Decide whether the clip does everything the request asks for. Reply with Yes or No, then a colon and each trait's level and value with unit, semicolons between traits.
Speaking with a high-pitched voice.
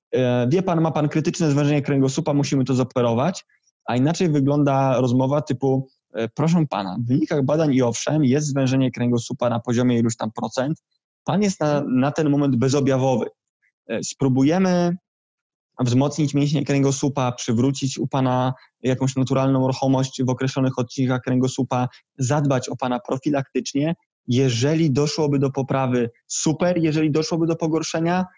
No: low, 135 Hz